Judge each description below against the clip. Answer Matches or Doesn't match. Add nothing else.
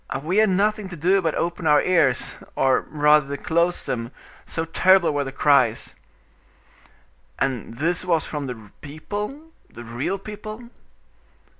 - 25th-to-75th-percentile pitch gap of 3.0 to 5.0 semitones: Doesn't match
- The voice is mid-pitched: Matches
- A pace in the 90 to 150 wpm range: Matches